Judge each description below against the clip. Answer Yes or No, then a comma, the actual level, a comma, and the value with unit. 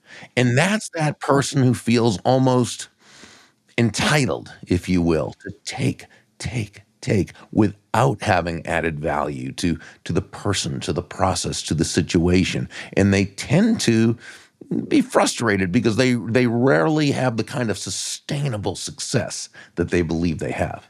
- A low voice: Yes, low, 110 Hz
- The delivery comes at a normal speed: Yes, average, 145 wpm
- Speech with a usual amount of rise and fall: No, wide, 6.2 semitones